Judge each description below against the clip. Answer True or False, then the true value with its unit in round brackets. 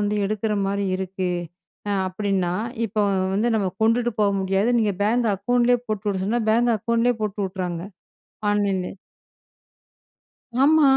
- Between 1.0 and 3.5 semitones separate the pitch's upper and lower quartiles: True (3.1 semitones)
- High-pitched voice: True (210 Hz)